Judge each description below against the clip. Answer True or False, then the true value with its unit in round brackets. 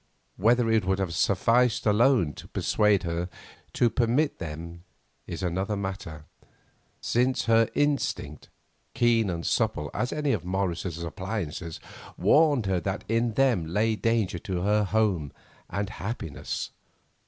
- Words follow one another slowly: True (130 wpm)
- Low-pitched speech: True (100 Hz)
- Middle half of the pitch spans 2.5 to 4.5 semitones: False (4.9 semitones)